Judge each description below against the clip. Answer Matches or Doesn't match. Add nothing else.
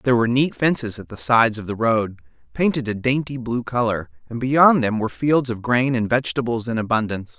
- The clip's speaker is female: Doesn't match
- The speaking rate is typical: Doesn't match